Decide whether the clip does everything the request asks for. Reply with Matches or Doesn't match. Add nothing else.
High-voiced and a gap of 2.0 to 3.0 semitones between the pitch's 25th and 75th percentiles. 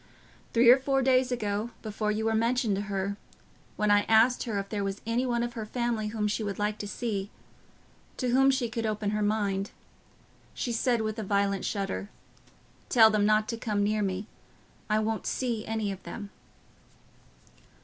Matches